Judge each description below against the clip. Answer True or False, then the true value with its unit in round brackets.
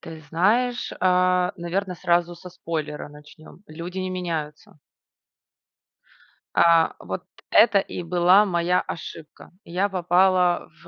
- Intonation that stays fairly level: True (1.8 semitones)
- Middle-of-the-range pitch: True (175 Hz)